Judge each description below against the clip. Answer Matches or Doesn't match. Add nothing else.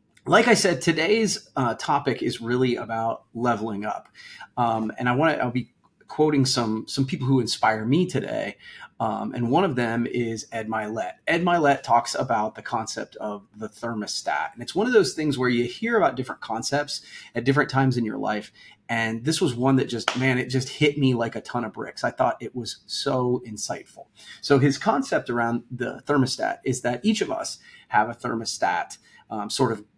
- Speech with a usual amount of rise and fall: Matches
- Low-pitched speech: Matches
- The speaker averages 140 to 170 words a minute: Doesn't match